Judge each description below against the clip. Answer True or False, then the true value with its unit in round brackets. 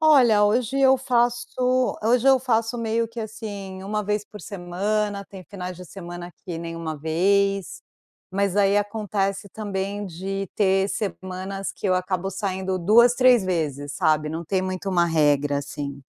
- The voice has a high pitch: True (195 Hz)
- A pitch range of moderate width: True (3.0 semitones)